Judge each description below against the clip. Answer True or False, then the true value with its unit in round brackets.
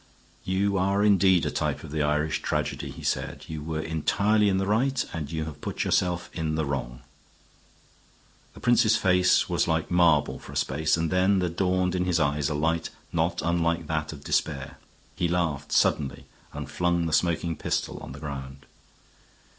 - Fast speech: False (180 wpm)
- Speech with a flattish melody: False (3.3 semitones)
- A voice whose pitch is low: True (80 Hz)